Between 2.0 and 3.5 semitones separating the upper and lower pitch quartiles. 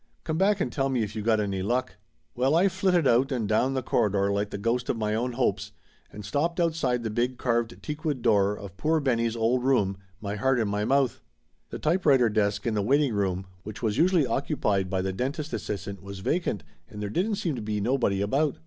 No: average, 5.1 semitones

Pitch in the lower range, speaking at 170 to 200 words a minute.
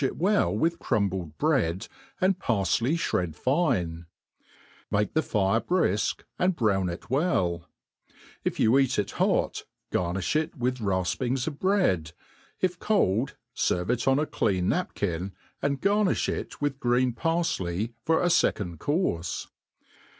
No: low, 120 Hz; average, 140 wpm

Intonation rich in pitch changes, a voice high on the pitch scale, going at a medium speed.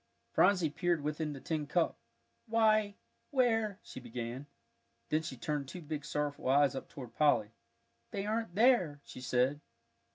No: wide, 6.4 semitones; medium, 150 Hz; average, 155 wpm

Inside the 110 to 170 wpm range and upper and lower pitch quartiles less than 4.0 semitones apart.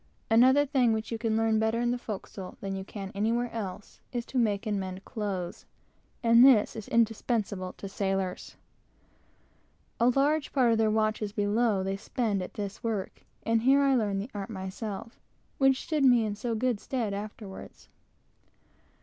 Yes: average, 165 wpm; average, 3.2 semitones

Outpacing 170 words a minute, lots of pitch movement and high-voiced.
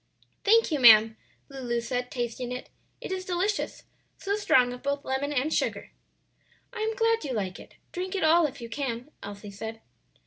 Yes: average, 180 wpm; wide, 7.3 semitones; very high, 265 Hz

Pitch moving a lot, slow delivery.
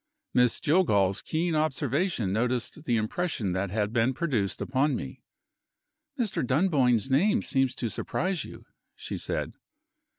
Yes: wide, 6.2 semitones; slow, 130 wpm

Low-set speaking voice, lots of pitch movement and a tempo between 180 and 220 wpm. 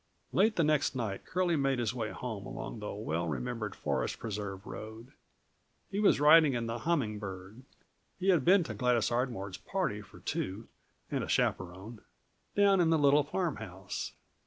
No: low, 120 Hz; wide, 6.8 semitones; average, 165 wpm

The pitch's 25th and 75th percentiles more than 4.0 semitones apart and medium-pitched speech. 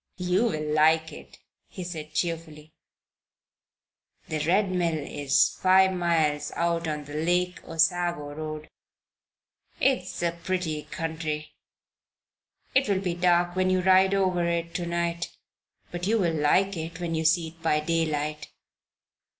No: narrow, 2.5 semitones; medium, 170 Hz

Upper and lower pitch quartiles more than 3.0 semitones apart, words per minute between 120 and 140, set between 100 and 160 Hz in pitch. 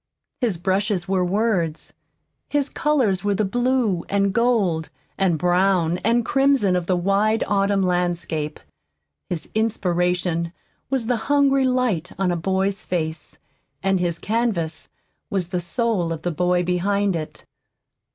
No: average, 4.1 semitones; slow, 135 wpm; high, 190 Hz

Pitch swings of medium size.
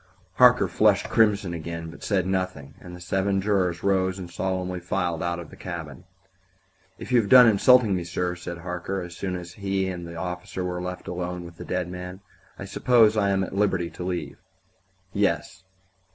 No: narrow, 1.8 semitones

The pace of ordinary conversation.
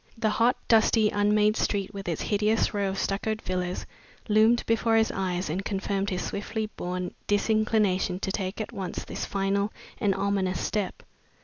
Yes: average, 165 wpm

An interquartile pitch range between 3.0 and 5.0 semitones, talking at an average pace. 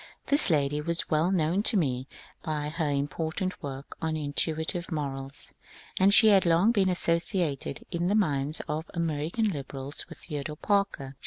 Yes: average, 4.1 semitones; average, 160 wpm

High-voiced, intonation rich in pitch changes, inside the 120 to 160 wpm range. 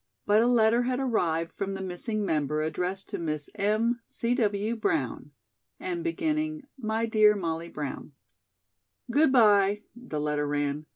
Yes: high, 210 Hz; wide, 6.6 semitones; average, 150 wpm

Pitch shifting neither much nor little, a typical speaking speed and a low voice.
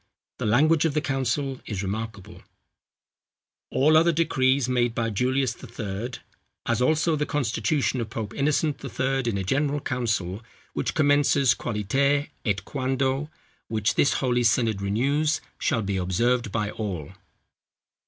Yes: average, 4.5 semitones; average, 145 wpm; low, 125 Hz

